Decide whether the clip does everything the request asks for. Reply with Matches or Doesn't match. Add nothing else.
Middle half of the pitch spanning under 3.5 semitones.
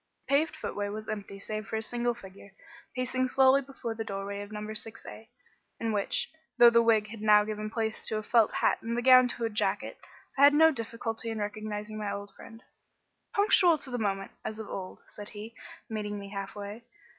Matches